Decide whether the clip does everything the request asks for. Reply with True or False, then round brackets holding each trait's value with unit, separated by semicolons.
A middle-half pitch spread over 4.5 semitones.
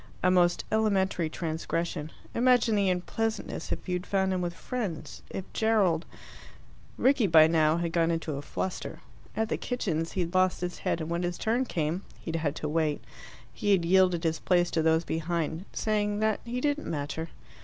False (4.1 semitones)